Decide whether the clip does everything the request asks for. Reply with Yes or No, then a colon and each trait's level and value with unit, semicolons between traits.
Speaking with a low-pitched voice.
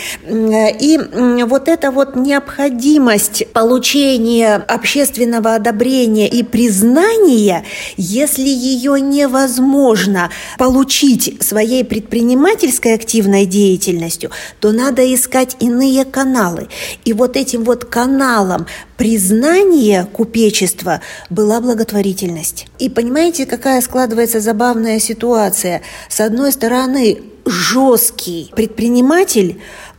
No: high, 235 Hz